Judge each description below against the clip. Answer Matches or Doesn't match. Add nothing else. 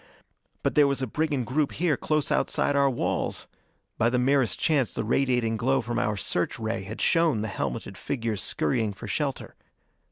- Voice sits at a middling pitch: Doesn't match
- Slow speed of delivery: Doesn't match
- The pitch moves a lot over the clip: Doesn't match